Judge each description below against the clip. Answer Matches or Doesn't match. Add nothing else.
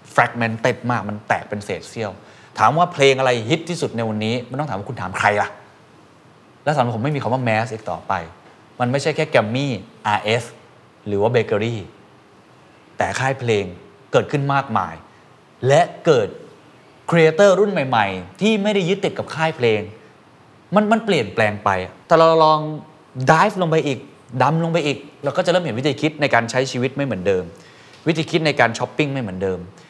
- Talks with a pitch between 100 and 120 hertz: Doesn't match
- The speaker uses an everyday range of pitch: Doesn't match